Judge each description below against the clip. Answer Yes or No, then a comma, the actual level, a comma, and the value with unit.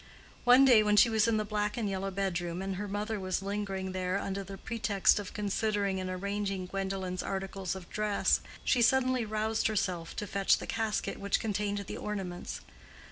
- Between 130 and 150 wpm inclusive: No, average, 185 wpm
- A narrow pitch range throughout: Yes, narrow, 1.9 semitones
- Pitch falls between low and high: No, high, 200 Hz